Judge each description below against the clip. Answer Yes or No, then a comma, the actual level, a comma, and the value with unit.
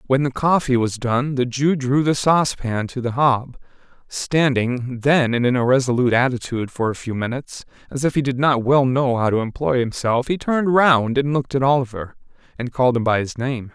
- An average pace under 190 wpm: No, fast, 205 wpm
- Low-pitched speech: Yes, low, 130 Hz